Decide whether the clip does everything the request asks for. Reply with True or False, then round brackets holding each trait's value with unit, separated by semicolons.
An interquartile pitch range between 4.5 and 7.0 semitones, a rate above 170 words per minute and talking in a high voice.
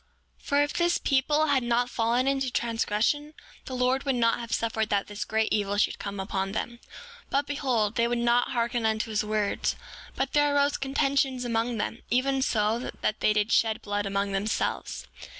False (3.9 semitones; 190 wpm; 235 Hz)